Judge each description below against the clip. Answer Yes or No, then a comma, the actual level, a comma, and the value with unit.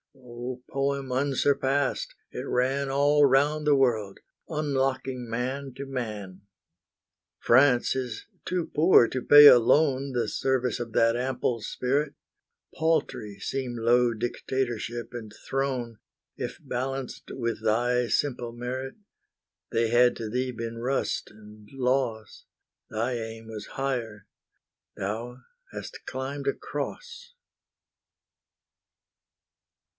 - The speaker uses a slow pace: Yes, slow, 110 wpm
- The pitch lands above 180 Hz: No, low, 125 Hz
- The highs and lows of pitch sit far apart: No, average, 2.7 semitones